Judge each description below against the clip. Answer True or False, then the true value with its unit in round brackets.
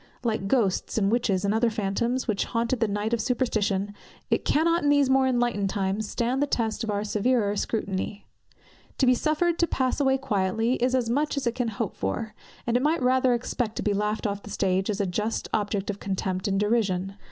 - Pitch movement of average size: True (3.9 semitones)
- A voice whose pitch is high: True (225 Hz)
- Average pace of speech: False (210 wpm)